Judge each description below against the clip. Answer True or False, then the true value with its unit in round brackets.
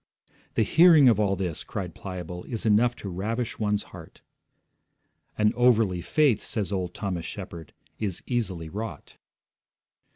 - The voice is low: True (105 Hz)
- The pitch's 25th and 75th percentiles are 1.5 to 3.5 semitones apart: False (4.0 semitones)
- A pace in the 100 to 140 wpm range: True (135 wpm)